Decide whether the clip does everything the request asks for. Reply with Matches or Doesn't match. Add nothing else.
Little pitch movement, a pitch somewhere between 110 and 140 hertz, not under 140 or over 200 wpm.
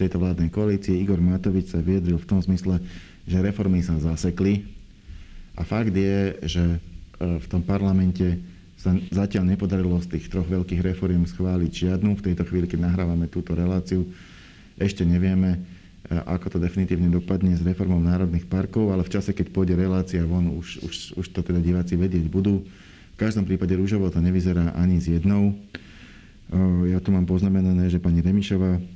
Doesn't match